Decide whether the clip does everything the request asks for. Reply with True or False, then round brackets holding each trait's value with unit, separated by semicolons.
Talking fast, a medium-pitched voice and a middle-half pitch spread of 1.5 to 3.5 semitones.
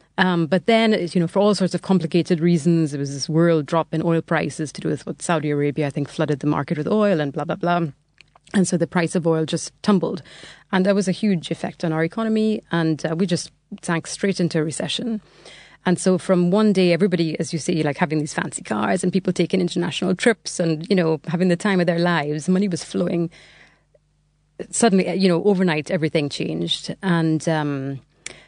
True (215 wpm; 170 Hz; 2.8 semitones)